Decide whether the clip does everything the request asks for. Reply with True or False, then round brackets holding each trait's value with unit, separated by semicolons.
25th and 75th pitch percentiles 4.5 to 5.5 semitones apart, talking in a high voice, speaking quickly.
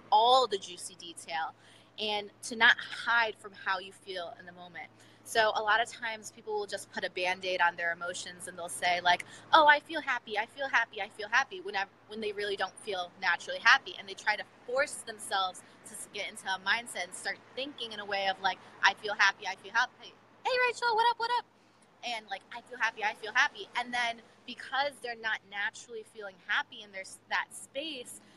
True (5.1 semitones; 210 Hz; 220 wpm)